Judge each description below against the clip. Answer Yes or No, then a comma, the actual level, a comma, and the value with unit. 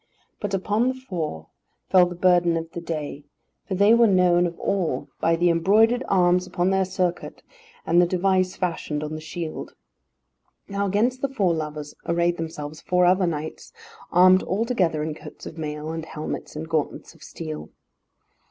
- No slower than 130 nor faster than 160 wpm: No, average, 170 wpm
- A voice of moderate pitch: Yes, medium, 175 Hz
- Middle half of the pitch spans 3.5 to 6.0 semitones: No, average, 3.1 semitones